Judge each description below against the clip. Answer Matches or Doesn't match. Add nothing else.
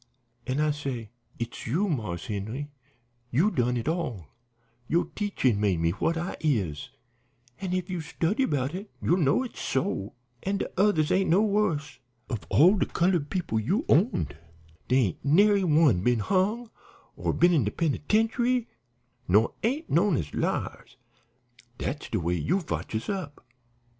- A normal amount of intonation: Doesn't match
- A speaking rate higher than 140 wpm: Matches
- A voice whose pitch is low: Doesn't match